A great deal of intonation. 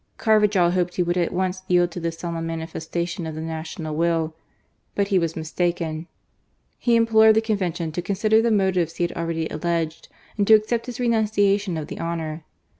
No: average, 3.8 semitones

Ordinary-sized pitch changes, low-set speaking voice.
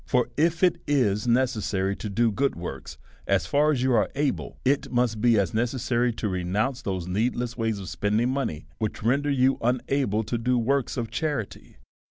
Yes: average, 3.9 semitones; low, 120 Hz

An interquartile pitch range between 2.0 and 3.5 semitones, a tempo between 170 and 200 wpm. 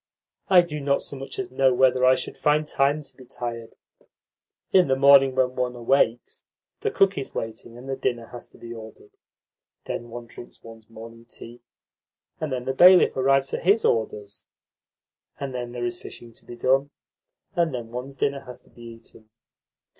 Yes: average, 2.8 semitones; average, 185 wpm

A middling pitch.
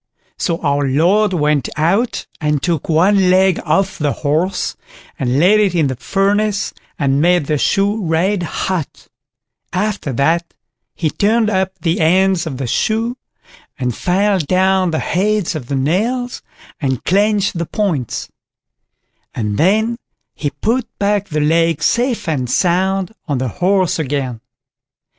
Yes: medium, 180 Hz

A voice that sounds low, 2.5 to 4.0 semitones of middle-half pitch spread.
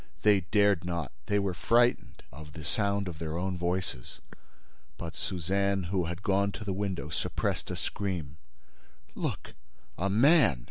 Yes: very low, 95 Hz; average, 3.4 semitones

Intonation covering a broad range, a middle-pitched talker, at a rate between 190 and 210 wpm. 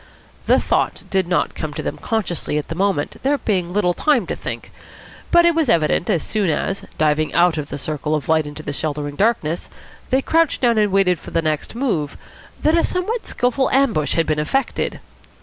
Yes: wide, 8.1 semitones; medium, 180 Hz; average, 200 wpm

